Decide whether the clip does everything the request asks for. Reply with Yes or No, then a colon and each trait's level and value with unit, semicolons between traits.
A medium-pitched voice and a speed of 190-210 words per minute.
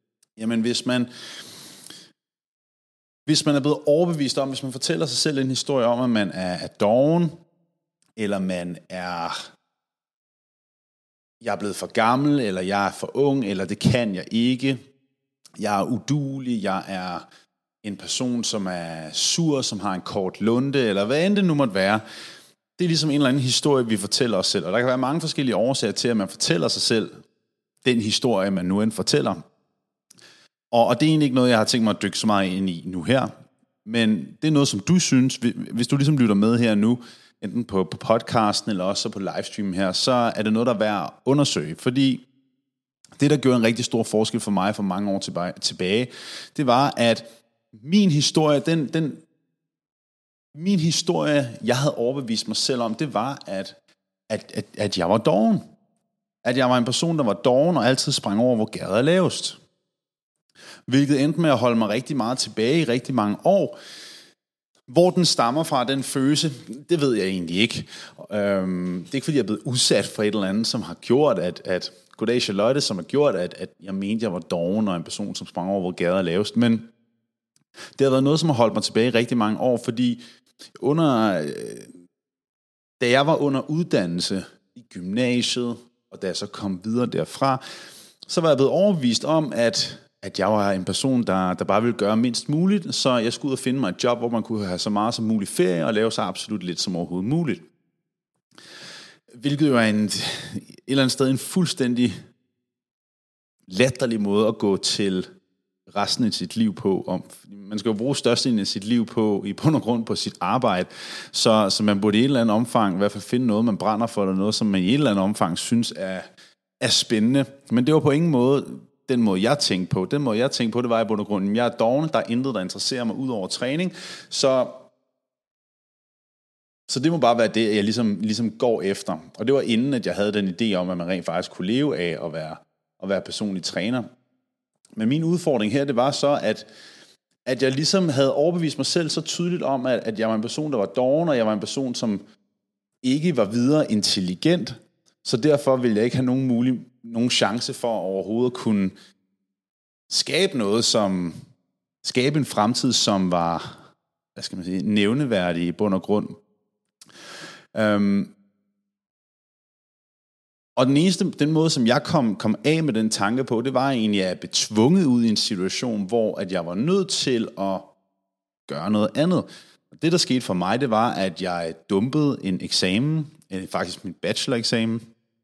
No: low, 120 Hz; average, 200 wpm